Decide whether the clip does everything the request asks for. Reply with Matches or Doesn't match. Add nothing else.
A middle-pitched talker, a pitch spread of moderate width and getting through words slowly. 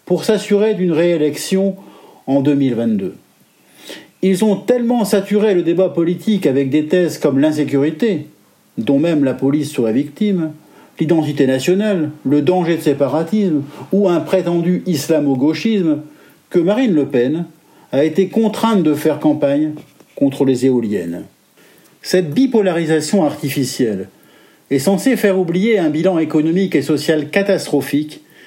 Matches